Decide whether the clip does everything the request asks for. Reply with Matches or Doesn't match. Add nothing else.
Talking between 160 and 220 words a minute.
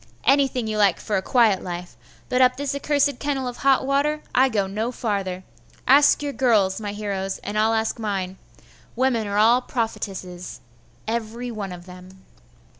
Matches